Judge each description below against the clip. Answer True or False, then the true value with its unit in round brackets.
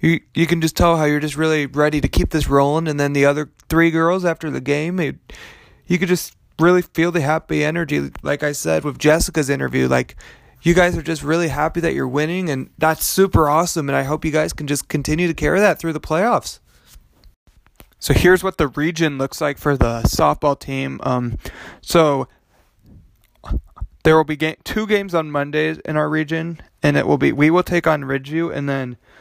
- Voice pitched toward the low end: False (155 Hz)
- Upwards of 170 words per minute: True (205 wpm)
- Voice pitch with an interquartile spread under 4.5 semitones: True (2.6 semitones)